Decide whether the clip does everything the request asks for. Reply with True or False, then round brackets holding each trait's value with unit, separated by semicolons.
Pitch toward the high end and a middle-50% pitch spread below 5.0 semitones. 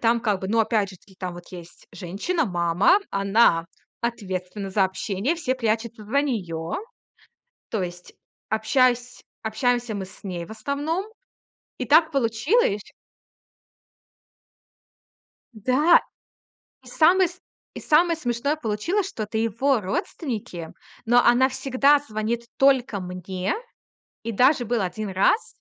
False (225 Hz; 5.5 semitones)